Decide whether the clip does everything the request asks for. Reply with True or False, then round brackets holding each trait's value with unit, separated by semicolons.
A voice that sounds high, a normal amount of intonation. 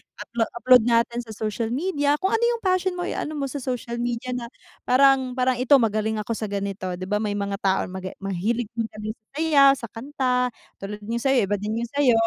True (235 Hz; 4.2 semitones)